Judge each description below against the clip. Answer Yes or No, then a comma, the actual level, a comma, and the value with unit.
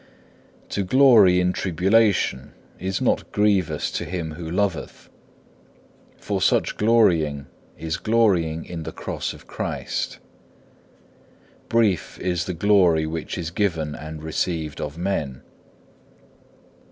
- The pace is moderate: No, slow, 115 wpm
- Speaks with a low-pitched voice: Yes, very low, 90 Hz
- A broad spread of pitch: No, average, 4.1 semitones